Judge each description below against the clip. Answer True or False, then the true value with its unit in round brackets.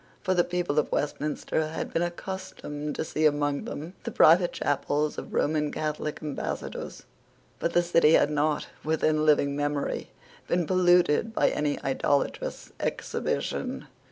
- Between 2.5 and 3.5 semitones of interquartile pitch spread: True (2.8 semitones)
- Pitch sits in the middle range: True (155 Hz)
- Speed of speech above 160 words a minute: False (140 wpm)